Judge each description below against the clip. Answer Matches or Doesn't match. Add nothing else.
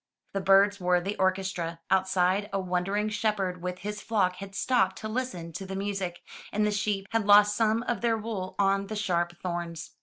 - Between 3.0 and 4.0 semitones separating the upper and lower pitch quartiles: Doesn't match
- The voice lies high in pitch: Matches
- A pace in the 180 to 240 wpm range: Matches